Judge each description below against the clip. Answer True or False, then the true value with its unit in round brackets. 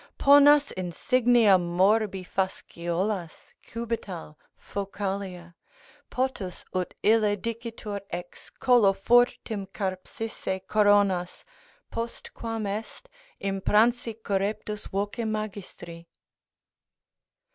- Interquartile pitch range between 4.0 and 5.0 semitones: False (3.3 semitones)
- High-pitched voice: True (205 Hz)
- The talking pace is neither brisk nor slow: False (70 wpm)